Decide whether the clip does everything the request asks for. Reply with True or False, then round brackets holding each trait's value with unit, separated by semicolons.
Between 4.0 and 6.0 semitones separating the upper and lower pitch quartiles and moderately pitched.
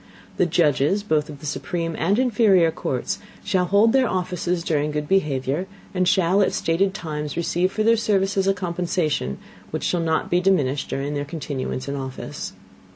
True (4.5 semitones; 170 Hz)